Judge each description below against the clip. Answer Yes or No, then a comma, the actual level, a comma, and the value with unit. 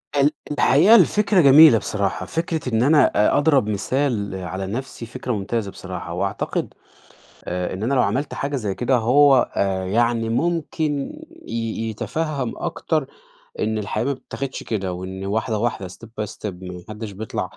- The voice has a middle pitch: No, low, 115 Hz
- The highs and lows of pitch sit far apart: Yes, wide, 5.9 semitones